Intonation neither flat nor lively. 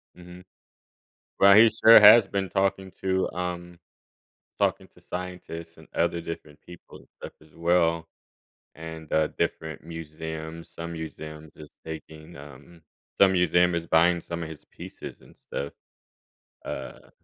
No: narrow, 2.0 semitones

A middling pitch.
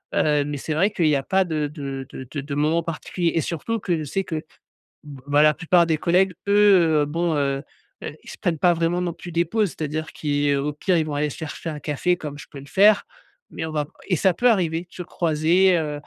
Yes: medium, 160 Hz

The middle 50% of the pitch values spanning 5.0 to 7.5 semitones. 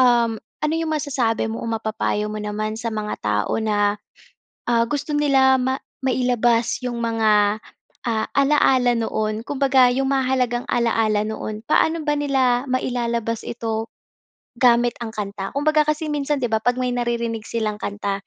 No: average, 3.2 semitones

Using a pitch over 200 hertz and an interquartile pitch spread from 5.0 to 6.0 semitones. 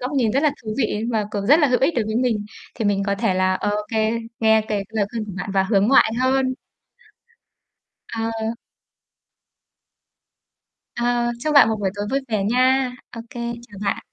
No: high, 225 Hz; average, 3.7 semitones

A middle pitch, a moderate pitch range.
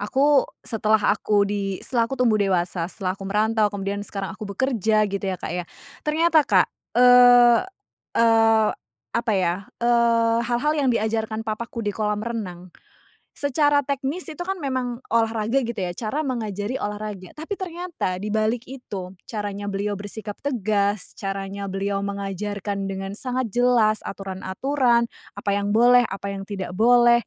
No: high, 215 Hz; average, 3.5 semitones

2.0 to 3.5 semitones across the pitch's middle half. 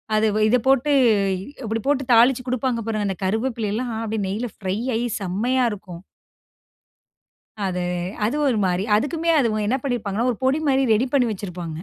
No: average, 4.1 semitones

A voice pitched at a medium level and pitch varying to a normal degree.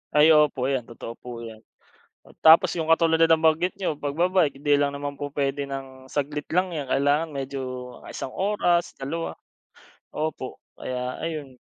Yes: medium, 145 Hz; average, 3.2 semitones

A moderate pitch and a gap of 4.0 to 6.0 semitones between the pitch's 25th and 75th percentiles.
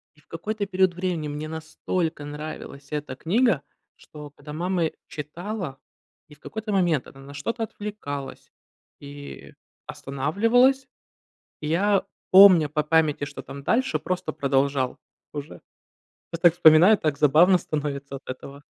Yes: medium, 155 Hz; average, 4.6 semitones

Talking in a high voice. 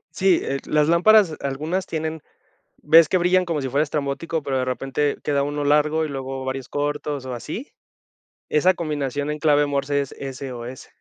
No: medium, 145 Hz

